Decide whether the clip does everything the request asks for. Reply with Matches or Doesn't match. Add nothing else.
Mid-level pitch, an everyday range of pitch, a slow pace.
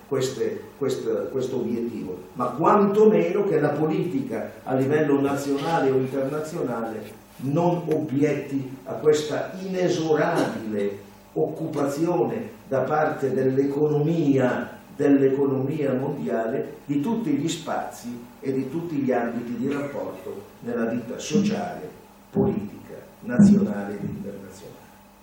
Matches